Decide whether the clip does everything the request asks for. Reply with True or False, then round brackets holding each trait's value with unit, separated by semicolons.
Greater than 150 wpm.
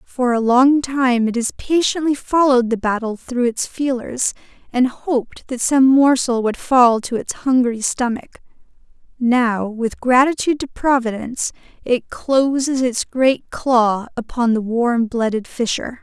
False (145 wpm)